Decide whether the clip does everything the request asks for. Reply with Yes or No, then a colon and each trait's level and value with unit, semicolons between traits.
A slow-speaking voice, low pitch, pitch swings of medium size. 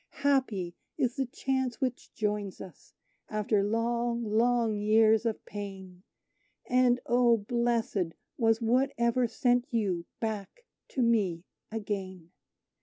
No: slow, 110 wpm; high, 225 Hz; average, 3.0 semitones